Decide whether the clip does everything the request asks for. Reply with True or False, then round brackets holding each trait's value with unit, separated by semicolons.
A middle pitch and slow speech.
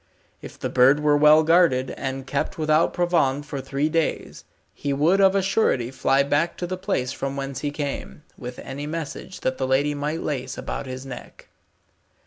False (145 Hz; 185 wpm)